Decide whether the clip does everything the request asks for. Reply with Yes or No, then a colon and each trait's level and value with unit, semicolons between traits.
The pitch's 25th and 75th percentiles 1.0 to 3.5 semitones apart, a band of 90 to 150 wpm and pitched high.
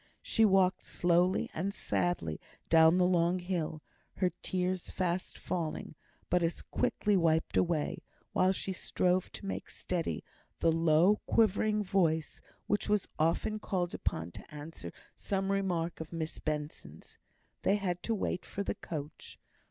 No: average, 2.9 semitones; average, 145 wpm; medium, 180 Hz